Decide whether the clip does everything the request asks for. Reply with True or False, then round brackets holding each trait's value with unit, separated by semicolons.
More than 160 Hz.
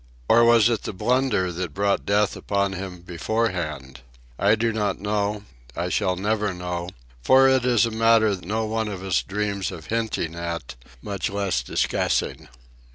False (100 Hz)